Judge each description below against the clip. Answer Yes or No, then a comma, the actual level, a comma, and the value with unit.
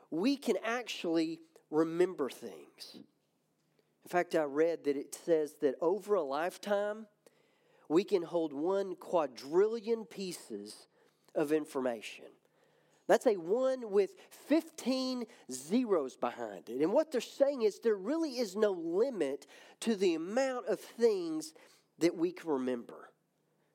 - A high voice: Yes, high, 230 Hz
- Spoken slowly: Yes, slow, 130 wpm